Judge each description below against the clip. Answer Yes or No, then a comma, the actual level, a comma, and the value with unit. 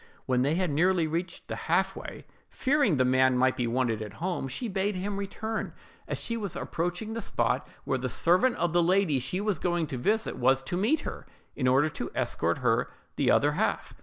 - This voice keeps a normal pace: No, fast, 210 wpm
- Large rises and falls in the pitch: Yes, wide, 7.2 semitones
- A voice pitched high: No, medium, 170 Hz